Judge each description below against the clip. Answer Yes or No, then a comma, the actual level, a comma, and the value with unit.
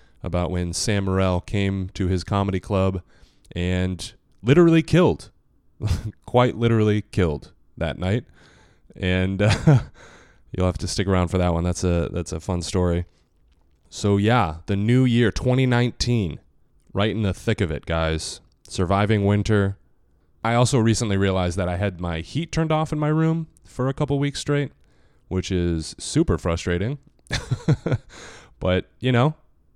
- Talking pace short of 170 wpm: Yes, average, 150 wpm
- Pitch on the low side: Yes, very low, 95 Hz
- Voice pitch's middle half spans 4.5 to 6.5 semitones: Yes, average, 5.2 semitones